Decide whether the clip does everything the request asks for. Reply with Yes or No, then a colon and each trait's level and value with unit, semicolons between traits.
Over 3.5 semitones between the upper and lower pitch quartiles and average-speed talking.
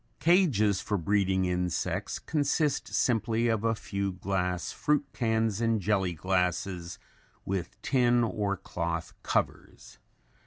No: average, 4.0 semitones; slow, 115 wpm